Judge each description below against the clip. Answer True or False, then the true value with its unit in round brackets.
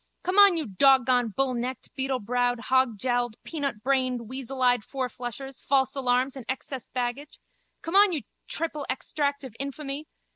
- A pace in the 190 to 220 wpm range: False (135 wpm)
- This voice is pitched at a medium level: False (260 Hz)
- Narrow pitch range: True (2.2 semitones)